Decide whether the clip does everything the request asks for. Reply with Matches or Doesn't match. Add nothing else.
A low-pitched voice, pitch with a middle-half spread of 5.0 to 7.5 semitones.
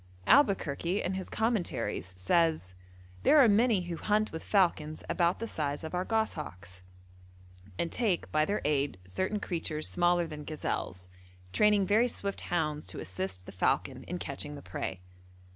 Doesn't match